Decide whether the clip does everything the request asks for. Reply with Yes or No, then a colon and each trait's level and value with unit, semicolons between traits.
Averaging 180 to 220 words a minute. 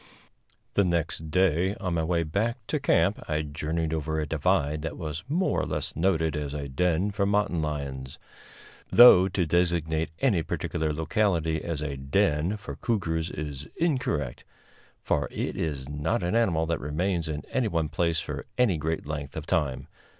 No: average, 170 wpm